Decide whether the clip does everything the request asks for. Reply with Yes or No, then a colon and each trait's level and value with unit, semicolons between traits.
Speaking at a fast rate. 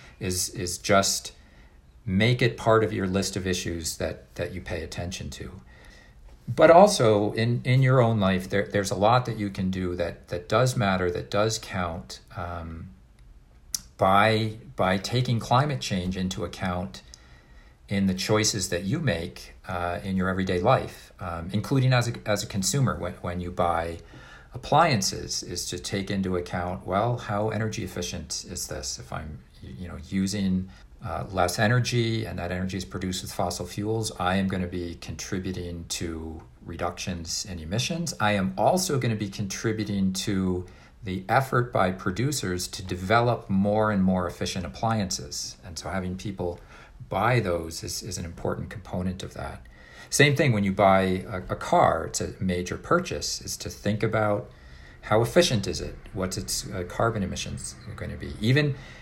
No: average, 170 wpm